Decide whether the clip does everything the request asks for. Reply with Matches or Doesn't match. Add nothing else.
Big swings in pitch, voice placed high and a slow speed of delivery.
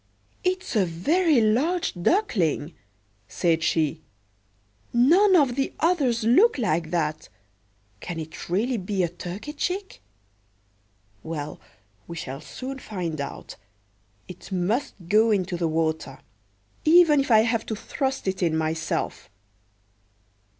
Matches